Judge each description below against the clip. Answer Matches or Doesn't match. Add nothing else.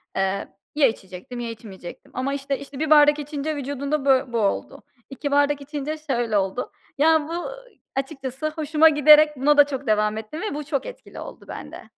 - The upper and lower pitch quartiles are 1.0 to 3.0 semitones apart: Doesn't match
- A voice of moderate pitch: Doesn't match